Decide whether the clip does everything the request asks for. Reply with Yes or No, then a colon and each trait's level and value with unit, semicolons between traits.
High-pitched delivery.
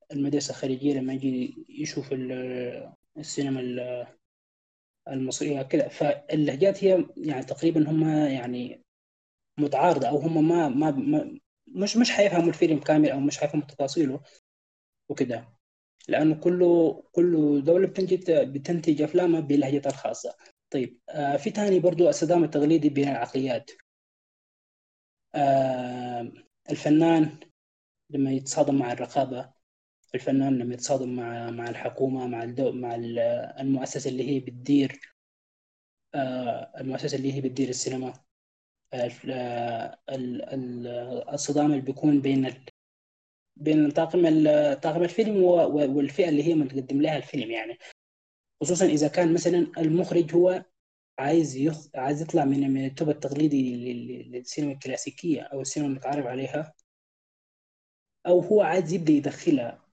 No: medium, 140 Hz